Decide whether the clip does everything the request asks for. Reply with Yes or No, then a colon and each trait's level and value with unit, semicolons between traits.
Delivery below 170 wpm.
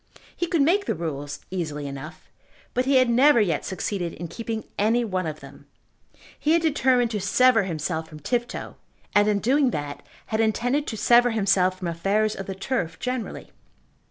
No: average, 180 wpm